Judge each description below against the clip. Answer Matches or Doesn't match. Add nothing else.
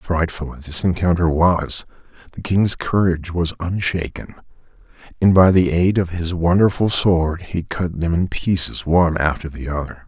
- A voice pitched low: Matches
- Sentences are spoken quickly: Doesn't match